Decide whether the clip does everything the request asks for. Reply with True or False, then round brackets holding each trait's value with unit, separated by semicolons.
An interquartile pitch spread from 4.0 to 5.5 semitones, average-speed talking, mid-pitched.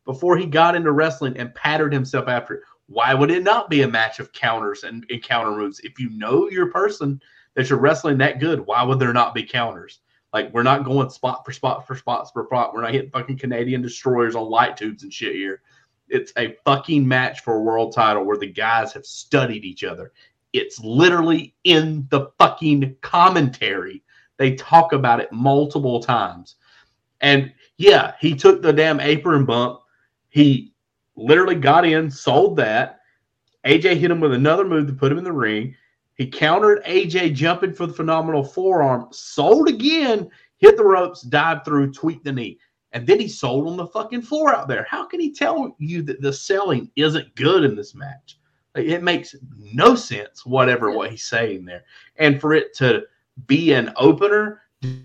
True (5.2 semitones; 185 wpm; 145 Hz)